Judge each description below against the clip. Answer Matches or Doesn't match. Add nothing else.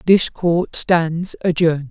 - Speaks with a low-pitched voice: Doesn't match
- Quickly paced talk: Doesn't match